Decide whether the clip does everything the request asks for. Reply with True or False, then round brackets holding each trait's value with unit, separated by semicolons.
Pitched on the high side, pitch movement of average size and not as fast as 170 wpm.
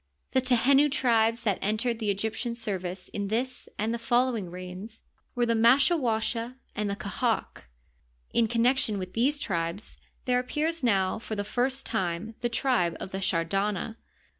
True (225 Hz; 3.8 semitones; 160 wpm)